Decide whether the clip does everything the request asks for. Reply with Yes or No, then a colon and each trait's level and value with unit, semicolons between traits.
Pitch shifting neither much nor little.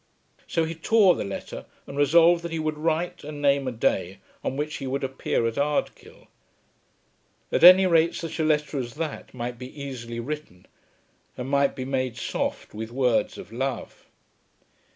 Yes: average, 4.1 semitones